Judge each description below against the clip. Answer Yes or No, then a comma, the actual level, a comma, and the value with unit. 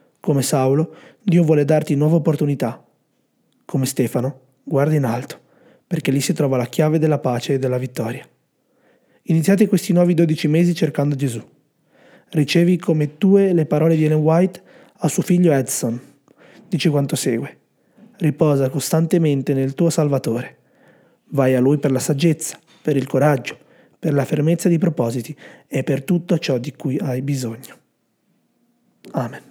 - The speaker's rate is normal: Yes, average, 150 wpm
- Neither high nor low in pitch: Yes, medium, 150 Hz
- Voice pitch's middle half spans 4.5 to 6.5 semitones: No, average, 3.8 semitones